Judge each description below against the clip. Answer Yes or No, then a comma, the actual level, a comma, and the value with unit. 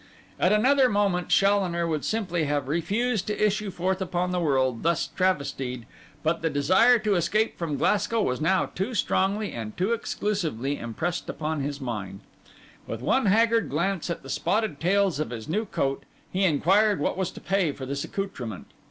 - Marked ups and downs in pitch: Yes, wide, 6.0 semitones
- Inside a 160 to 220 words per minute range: Yes, average, 175 wpm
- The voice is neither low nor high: Yes, medium, 180 Hz